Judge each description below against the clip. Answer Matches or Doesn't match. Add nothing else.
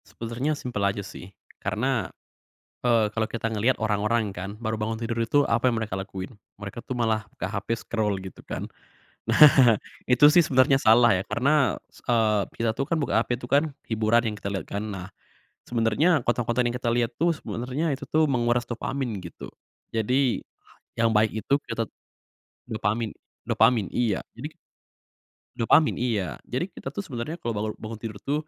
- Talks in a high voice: Doesn't match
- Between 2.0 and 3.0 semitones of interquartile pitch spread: Matches